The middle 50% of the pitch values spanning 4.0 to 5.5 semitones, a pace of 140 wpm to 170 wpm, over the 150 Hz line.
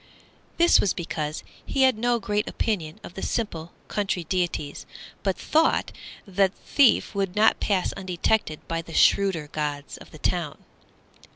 Yes: average, 4.5 semitones; average, 155 wpm; high, 190 Hz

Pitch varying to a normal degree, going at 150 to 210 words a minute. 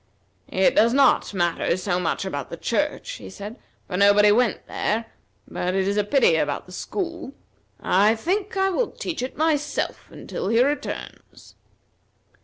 No: wide, 7.7 semitones; average, 160 wpm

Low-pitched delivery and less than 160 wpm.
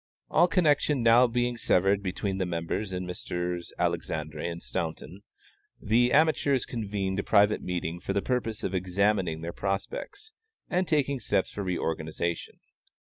Yes: low, 100 Hz; average, 140 wpm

